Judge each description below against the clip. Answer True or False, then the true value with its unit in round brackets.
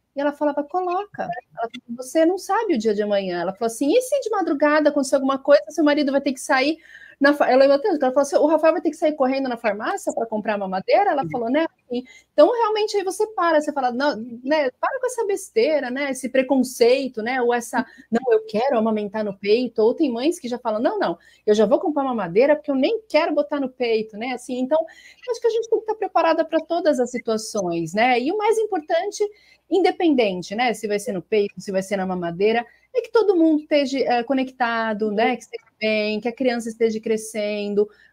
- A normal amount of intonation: False (6.0 semitones)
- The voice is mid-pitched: False (275 Hz)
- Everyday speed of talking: False (230 wpm)